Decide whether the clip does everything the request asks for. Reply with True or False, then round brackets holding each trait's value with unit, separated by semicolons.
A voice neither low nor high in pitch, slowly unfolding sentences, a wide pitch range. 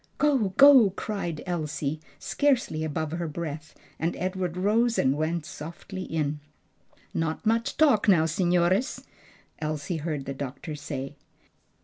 False (165 Hz; 125 wpm; 4.6 semitones)